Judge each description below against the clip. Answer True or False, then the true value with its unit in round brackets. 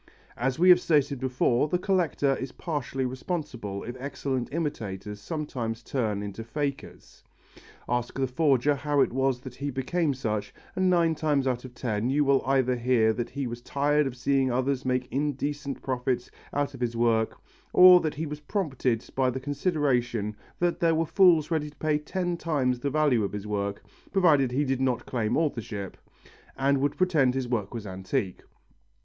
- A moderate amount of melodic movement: True (3.6 semitones)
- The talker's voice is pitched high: False (135 Hz)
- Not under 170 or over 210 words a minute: True (180 wpm)